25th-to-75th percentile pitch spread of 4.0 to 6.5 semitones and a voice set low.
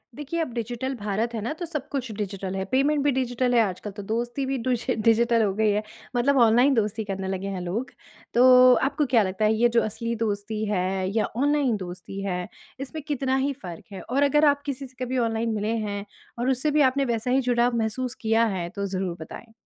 No: average, 4.4 semitones; high, 235 Hz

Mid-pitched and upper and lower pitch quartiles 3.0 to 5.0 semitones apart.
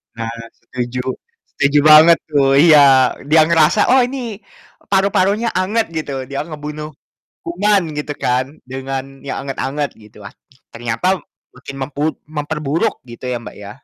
Yes: medium, 150 Hz; average, 4.2 semitones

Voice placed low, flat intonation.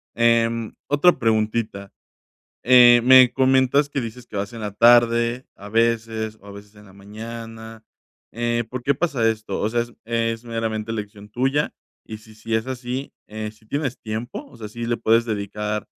Yes: low, 115 Hz; narrow, 1.9 semitones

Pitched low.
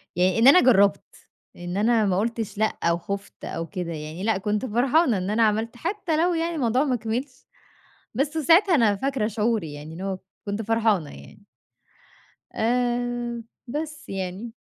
No: high, 225 Hz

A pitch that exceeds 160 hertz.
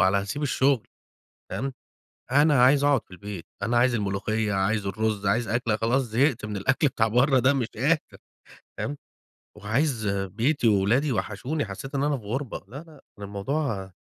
No: low, 115 Hz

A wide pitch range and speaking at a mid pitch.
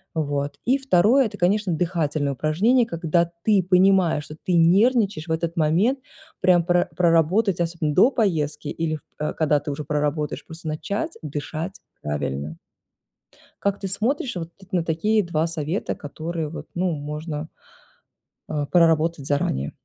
No: average, 3.8 semitones; medium, 165 Hz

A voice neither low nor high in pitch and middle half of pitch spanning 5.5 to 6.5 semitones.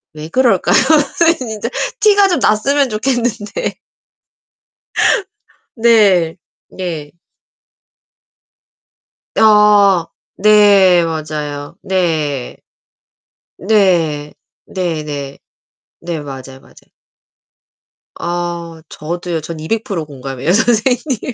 Yes: medium, 180 Hz; wide, 6.0 semitones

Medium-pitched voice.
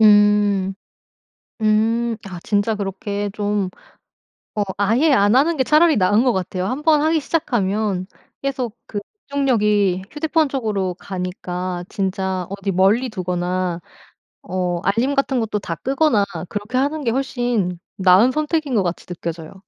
No: high, 210 Hz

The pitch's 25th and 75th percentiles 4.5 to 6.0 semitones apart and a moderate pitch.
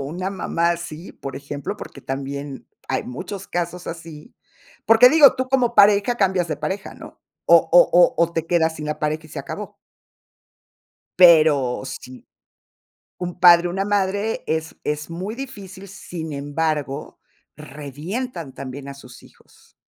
Yes: average, 5.0 semitones; medium, 170 Hz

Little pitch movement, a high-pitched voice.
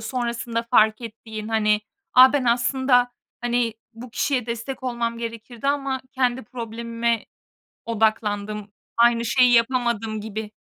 Yes: narrow, 1.9 semitones; high, 235 Hz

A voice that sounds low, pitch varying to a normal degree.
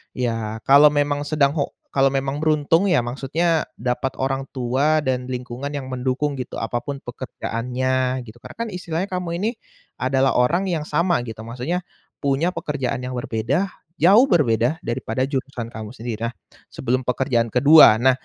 Yes: low, 130 Hz; average, 3.5 semitones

